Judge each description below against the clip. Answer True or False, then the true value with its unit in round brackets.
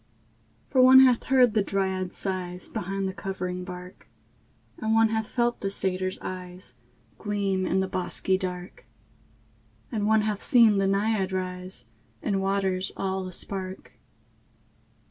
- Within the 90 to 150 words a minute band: True (140 wpm)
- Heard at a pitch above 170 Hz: True (190 Hz)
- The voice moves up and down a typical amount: False (2.2 semitones)